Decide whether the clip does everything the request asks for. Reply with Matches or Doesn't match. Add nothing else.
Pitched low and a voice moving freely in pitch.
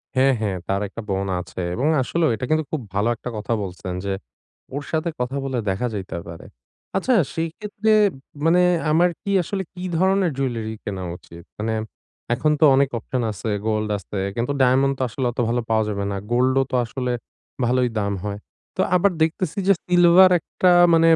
Matches